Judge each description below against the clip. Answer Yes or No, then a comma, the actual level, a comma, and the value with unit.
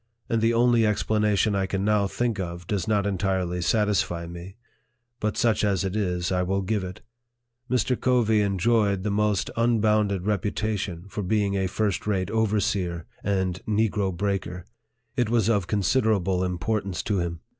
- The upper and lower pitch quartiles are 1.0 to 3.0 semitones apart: Yes, average, 2.7 semitones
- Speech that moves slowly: No, average, 165 wpm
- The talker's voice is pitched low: Yes, low, 100 Hz